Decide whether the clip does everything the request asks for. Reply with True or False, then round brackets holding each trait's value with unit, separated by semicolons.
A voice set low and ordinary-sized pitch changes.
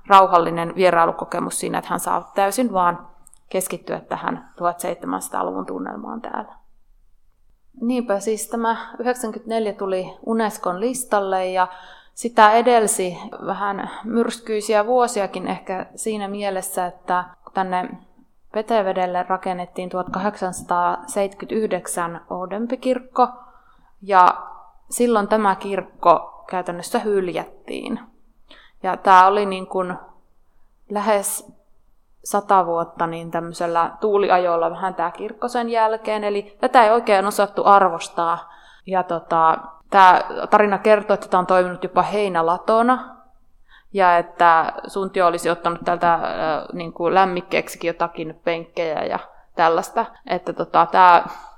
False (195 Hz; 3.4 semitones)